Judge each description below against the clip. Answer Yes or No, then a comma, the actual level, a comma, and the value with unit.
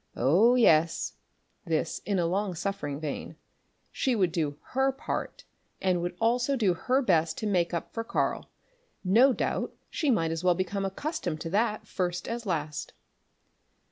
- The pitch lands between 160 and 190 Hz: Yes, medium, 185 Hz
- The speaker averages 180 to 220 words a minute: No, average, 155 wpm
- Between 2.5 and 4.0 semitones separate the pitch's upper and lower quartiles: No, wide, 5.4 semitones